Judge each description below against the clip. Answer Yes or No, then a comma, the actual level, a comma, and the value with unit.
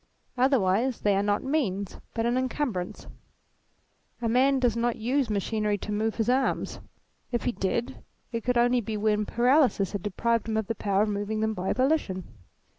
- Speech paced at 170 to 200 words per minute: Yes, average, 180 wpm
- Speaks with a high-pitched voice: Yes, high, 225 Hz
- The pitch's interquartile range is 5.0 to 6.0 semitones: No, average, 3.3 semitones